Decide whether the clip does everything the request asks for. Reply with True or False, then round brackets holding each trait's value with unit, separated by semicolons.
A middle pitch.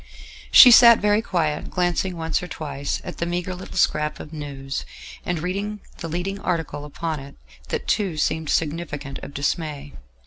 True (165 Hz)